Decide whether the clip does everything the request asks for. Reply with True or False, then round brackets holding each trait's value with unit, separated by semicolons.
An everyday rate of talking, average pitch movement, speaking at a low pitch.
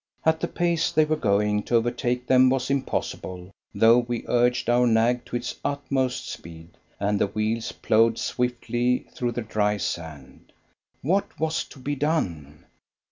True (155 wpm; 3.9 semitones; 120 Hz)